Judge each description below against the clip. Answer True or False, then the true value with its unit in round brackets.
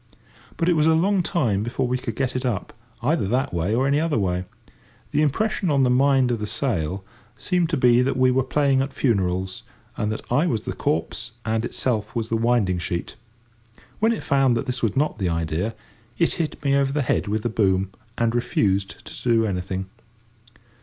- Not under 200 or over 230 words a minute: True (205 wpm)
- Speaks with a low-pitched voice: True (120 Hz)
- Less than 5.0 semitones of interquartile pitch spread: False (5.3 semitones)